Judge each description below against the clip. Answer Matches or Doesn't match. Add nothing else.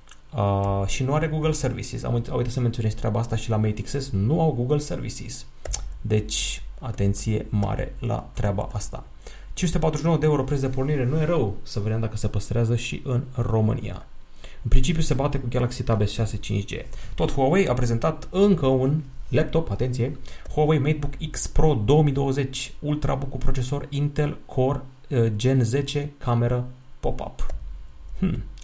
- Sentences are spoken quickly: Doesn't match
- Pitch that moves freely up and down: Doesn't match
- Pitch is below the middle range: Matches